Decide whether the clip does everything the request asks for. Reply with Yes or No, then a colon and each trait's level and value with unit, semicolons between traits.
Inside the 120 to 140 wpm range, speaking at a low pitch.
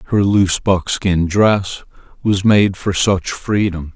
Yes: slow, 135 wpm; very low, 95 Hz